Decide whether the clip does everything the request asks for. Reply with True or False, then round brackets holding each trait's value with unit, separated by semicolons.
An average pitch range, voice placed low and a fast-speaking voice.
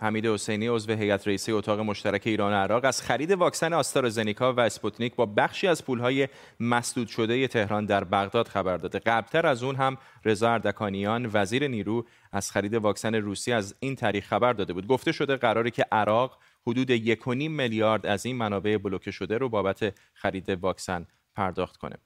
True (3.1 semitones; 110 Hz; 175 wpm)